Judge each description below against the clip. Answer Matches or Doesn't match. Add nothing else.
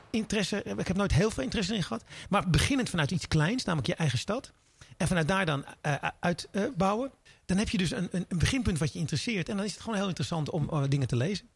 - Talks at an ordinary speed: Doesn't match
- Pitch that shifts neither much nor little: Matches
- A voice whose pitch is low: Doesn't match